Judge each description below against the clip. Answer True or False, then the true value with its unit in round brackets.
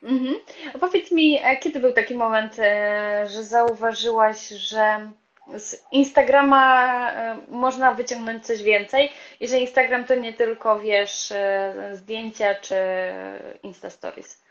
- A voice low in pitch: False (230 Hz)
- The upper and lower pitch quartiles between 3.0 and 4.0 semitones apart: True (3.7 semitones)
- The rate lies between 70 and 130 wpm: True (110 wpm)